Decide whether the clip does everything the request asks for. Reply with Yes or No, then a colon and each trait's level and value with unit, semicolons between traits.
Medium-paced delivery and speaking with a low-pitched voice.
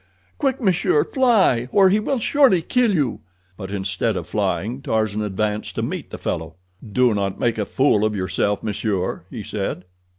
Yes: average, 170 wpm; low, 110 Hz